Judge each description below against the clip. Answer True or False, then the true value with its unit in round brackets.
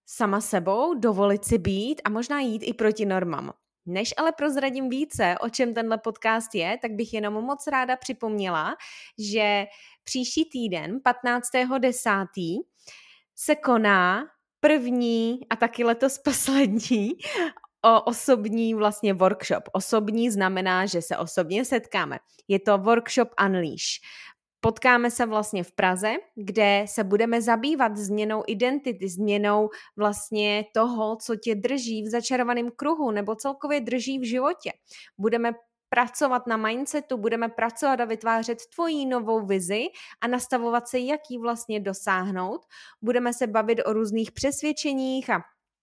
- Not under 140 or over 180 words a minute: False (130 wpm)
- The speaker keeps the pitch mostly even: False (3.3 semitones)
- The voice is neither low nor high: False (230 Hz)